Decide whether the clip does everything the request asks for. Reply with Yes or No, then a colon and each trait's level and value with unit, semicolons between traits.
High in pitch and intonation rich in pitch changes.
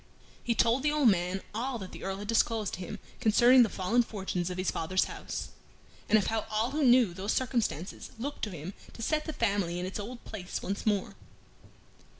No: high, 215 Hz; average, 4.2 semitones